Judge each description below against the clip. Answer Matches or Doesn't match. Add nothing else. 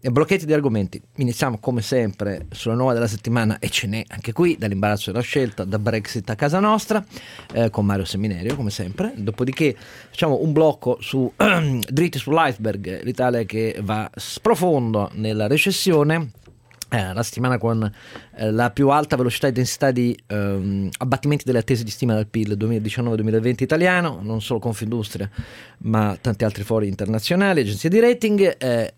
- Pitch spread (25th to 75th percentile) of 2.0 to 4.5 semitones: Matches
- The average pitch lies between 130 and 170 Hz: Doesn't match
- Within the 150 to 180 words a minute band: Matches